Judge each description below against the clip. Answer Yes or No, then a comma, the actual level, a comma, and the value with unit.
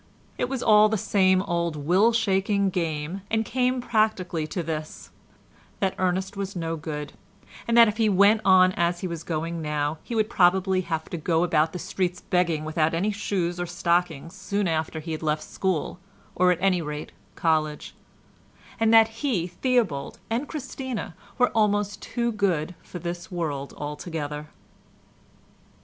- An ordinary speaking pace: Yes, average, 165 wpm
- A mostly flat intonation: No, average, 4.3 semitones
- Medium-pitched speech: Yes, medium, 180 Hz